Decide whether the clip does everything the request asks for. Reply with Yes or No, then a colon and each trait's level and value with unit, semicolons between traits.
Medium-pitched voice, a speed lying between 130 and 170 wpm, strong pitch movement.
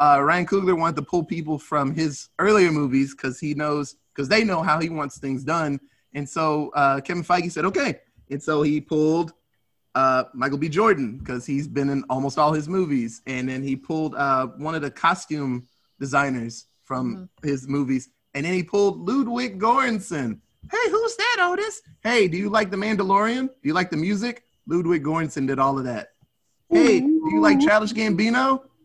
No: medium, 155 Hz; average, 190 wpm; wide, 6.3 semitones